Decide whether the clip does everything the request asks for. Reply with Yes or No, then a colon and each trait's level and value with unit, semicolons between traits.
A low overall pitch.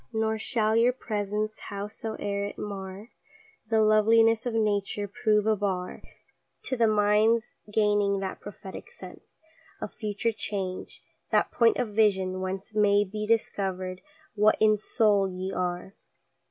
No: high, 210 Hz